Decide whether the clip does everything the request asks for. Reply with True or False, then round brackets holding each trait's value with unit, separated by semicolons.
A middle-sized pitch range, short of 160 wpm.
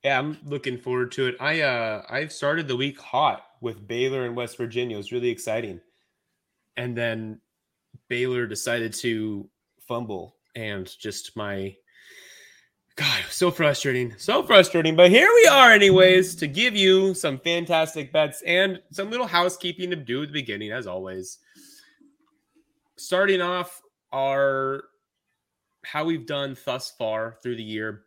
False (7.0 semitones; 150 wpm)